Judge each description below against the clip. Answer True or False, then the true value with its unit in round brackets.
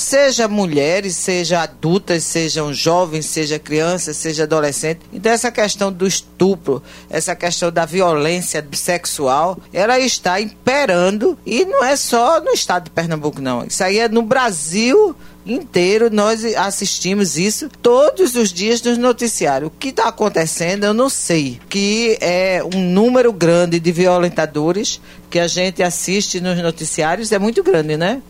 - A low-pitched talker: False (185 Hz)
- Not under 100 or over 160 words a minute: True (150 wpm)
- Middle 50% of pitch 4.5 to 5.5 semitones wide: True (5.2 semitones)